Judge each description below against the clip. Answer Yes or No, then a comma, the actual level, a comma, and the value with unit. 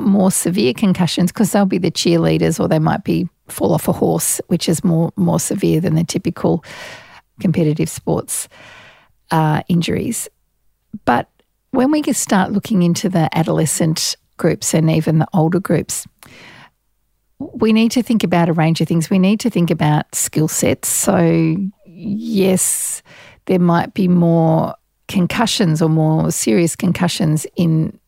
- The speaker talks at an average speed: Yes, average, 150 wpm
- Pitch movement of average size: Yes, average, 3.4 semitones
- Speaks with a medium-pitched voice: Yes, medium, 175 Hz